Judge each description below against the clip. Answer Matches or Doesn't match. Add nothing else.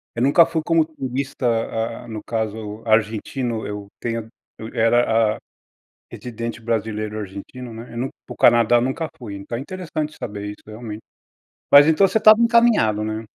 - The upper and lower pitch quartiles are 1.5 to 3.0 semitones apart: Doesn't match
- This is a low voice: Matches